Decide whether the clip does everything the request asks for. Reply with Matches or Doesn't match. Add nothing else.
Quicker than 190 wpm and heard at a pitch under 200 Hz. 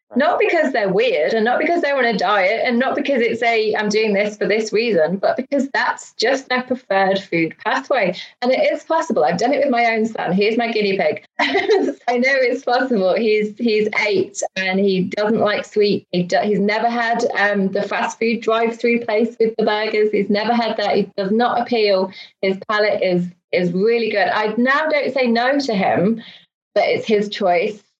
Doesn't match